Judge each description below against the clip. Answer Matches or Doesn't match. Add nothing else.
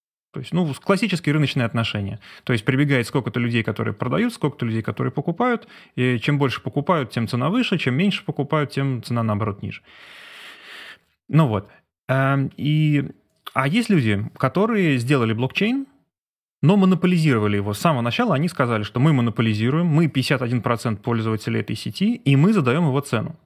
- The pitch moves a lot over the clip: Matches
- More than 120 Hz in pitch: Matches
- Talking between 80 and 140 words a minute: Doesn't match